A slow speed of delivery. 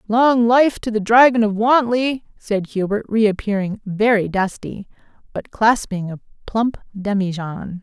Yes: slow, 130 wpm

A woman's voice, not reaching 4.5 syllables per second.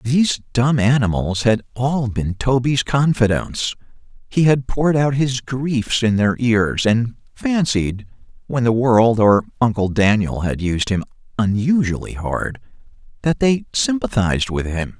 No: male; 4.1 syllables/s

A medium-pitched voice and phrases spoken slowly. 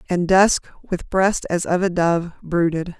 No: medium, 175 Hz; average, 180 wpm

